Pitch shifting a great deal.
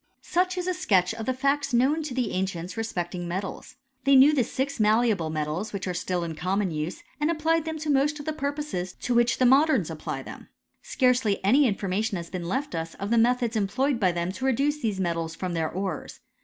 Yes: wide, 7.2 semitones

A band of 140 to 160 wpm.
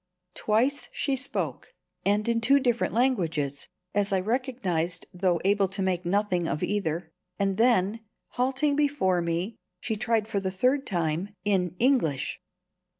Yes: average, 145 wpm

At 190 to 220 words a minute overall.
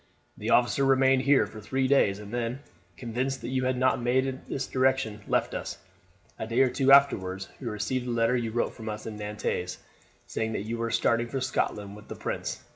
Yes: fast, 205 wpm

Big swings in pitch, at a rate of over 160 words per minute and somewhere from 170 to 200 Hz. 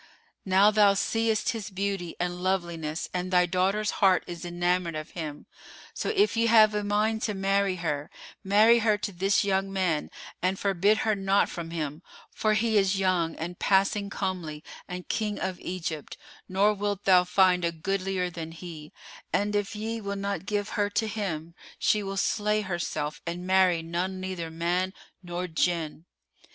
No: average, 2.8 semitones; average, 170 wpm; high, 190 Hz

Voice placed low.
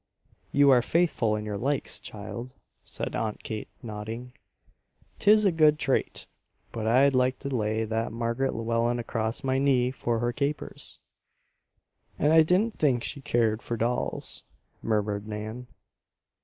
Yes: low, 120 Hz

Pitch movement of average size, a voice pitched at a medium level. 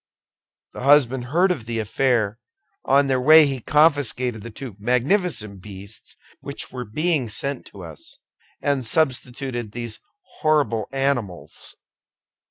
No: average, 4.3 semitones; low, 125 Hz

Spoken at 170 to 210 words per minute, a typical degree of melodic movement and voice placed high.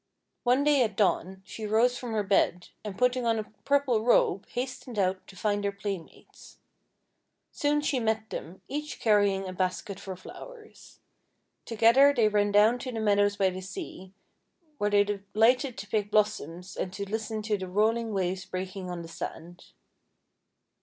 Yes: average, 175 wpm; average, 3.5 semitones; high, 210 Hz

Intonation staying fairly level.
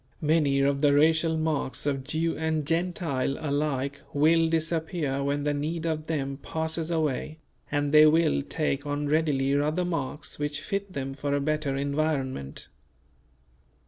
Yes: narrow, 2.2 semitones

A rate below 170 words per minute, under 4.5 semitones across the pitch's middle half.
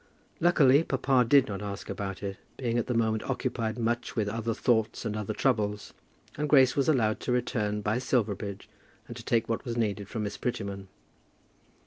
No: average, 180 wpm; average, 3.1 semitones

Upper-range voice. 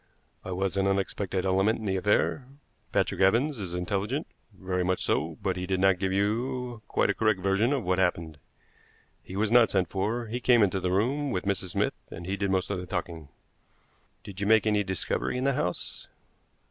No: very low, 95 Hz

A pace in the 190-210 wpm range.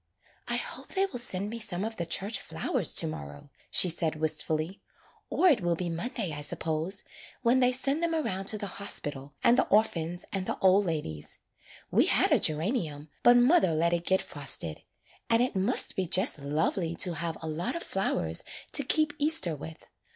Yes: average, 195 wpm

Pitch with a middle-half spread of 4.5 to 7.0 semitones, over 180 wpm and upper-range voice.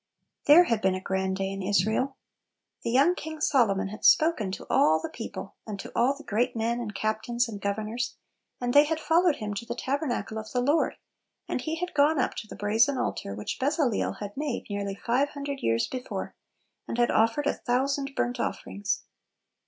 Yes: wide, 5.5 semitones; average, 200 wpm; high, 240 Hz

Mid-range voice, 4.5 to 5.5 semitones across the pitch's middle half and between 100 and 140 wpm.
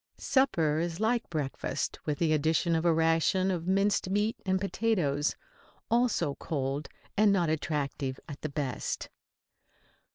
Yes: medium, 165 Hz; average, 4.8 semitones; slow, 135 wpm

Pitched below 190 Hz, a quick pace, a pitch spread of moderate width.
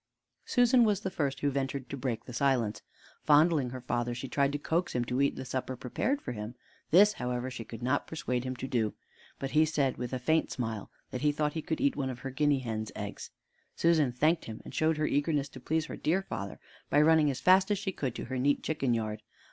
Yes: low, 135 Hz; fast, 235 wpm; average, 4.0 semitones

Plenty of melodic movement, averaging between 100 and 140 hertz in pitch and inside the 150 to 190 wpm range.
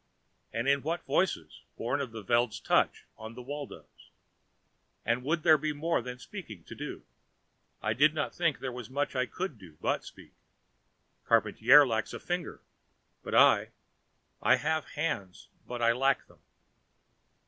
No: average, 4.8 semitones; low, 135 Hz; average, 160 wpm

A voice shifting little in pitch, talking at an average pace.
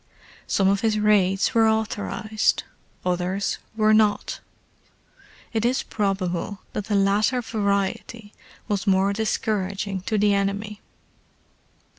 No: narrow, 1.7 semitones; slow, 110 wpm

